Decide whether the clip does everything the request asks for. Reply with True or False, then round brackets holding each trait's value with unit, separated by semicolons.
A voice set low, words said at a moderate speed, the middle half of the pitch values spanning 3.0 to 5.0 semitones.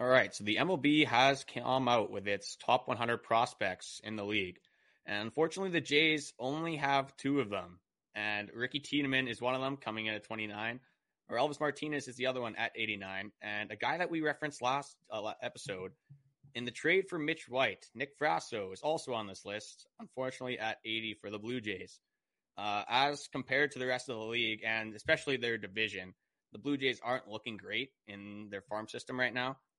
True (125 Hz; 195 wpm; 4.5 semitones)